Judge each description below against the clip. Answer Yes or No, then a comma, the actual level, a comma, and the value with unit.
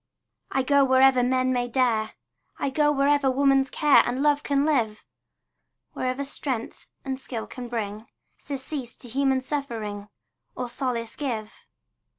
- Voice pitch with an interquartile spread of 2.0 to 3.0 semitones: Yes, average, 2.7 semitones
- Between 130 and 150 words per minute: Yes, average, 140 wpm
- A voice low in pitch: No, very high, 260 Hz